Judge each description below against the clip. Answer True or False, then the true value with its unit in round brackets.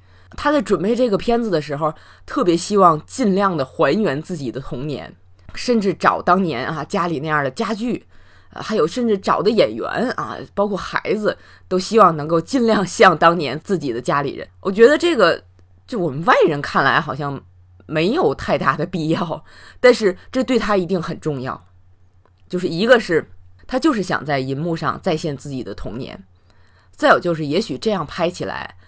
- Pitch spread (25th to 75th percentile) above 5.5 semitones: True (7.1 semitones)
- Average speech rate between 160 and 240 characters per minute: False (270 characters per minute)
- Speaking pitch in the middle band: True (165 Hz)